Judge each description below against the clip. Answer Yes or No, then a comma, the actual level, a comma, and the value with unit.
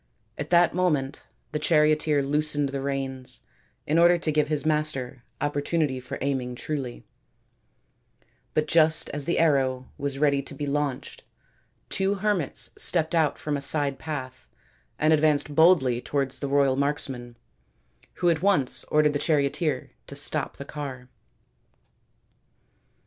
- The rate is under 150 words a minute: Yes, average, 140 wpm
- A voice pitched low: No, medium, 145 Hz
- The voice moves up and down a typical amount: No, narrow, 2.3 semitones